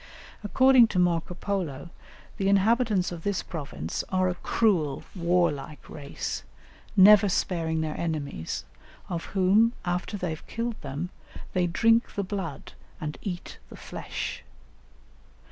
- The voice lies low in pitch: No, medium, 180 Hz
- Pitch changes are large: No, average, 3.9 semitones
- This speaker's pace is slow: Yes, slow, 130 wpm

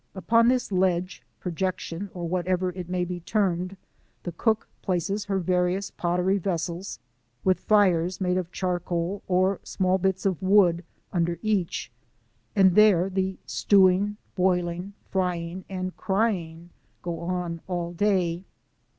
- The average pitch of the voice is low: No, medium, 185 Hz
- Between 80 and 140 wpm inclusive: Yes, slow, 135 wpm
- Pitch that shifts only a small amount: Yes, narrow, 1.8 semitones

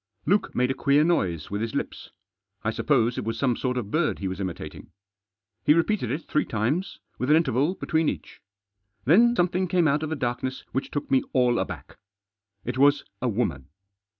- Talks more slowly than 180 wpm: No, average, 190 wpm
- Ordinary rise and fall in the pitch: Yes, average, 5.0 semitones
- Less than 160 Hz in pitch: Yes, low, 135 Hz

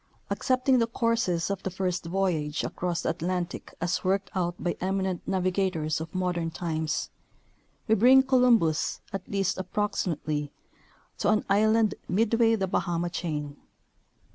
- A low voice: No, medium, 185 Hz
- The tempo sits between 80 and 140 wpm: Yes, slow, 135 wpm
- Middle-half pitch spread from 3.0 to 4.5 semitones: Yes, average, 3.7 semitones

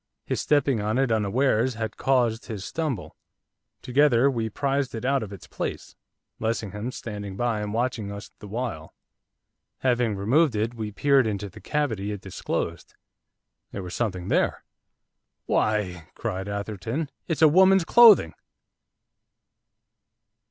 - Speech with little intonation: No, average, 4.6 semitones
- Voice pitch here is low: Yes, low, 115 Hz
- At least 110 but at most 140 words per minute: Yes, slow, 135 wpm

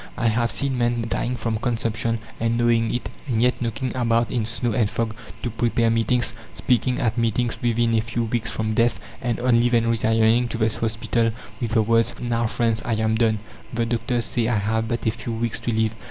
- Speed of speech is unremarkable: No, fast, 210 wpm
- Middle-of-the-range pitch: No, low, 115 Hz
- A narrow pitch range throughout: Yes, narrow, 1.1 semitones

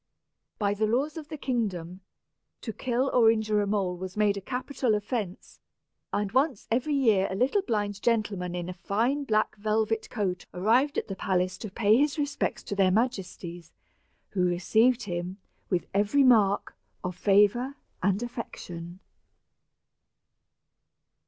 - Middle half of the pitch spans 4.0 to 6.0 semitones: Yes, average, 4.5 semitones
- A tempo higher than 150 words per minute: No, average, 145 wpm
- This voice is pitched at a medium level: No, high, 210 Hz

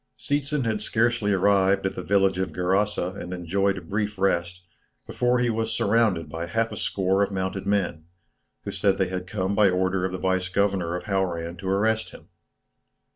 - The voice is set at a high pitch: No, very low, 95 Hz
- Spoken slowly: No, average, 185 wpm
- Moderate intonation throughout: No, narrow, 2.3 semitones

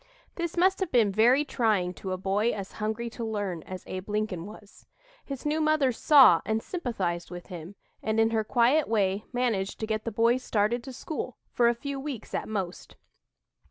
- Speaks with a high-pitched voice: Yes, high, 220 Hz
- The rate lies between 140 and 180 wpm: No, average, 195 wpm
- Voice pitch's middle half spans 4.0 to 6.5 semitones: Yes, average, 4.4 semitones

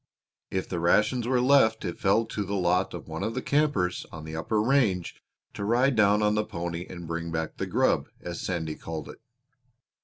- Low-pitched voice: Yes, very low, 95 Hz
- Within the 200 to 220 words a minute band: Yes, fast, 205 wpm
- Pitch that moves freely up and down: No, average, 4.7 semitones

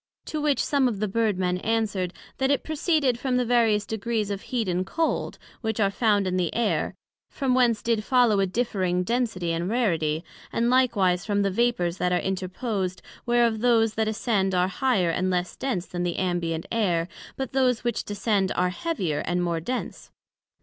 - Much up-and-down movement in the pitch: No, average, 4.8 semitones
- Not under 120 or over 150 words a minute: No, average, 185 wpm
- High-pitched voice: Yes, high, 210 Hz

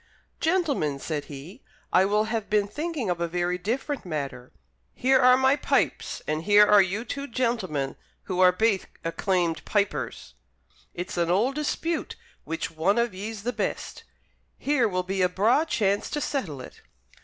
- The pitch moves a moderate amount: No, wide, 5.9 semitones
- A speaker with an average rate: Yes, average, 165 wpm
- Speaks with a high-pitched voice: Yes, high, 200 Hz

